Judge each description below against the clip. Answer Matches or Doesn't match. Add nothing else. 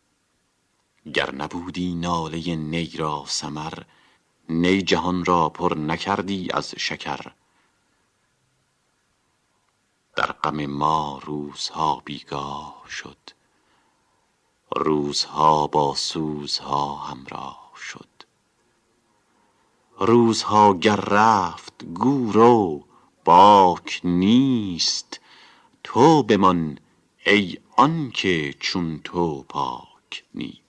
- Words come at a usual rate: Doesn't match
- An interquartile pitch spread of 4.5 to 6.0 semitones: Matches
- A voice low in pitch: Matches